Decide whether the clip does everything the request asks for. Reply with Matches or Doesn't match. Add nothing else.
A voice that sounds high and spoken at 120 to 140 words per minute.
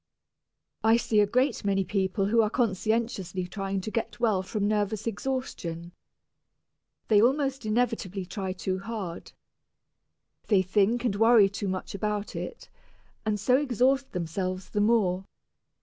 Matches